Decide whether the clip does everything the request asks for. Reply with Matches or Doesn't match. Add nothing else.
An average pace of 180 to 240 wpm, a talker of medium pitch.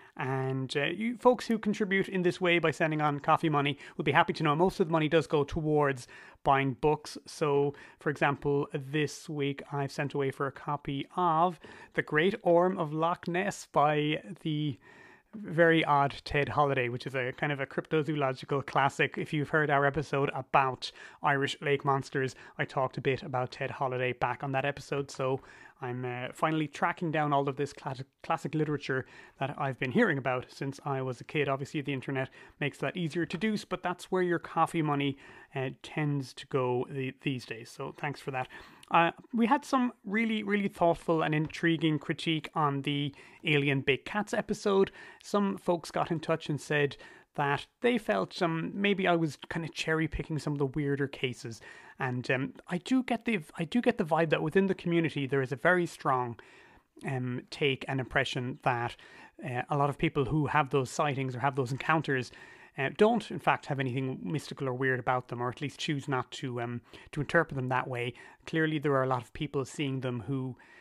Matches